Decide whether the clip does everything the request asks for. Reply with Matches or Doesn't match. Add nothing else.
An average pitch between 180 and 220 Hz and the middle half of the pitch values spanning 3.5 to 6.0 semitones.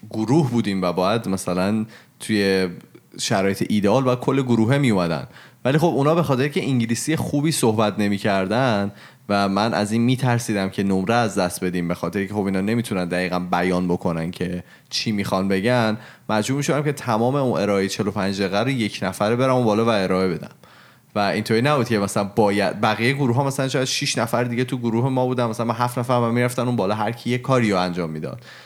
Doesn't match